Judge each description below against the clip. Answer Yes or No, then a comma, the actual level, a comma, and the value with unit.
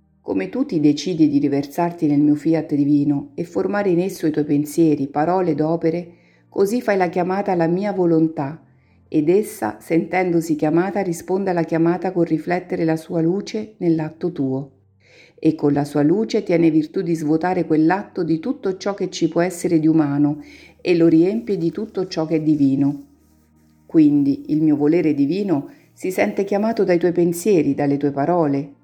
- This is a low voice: No, medium, 165 Hz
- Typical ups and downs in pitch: Yes, average, 3.5 semitones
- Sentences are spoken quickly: Yes, fast, 175 wpm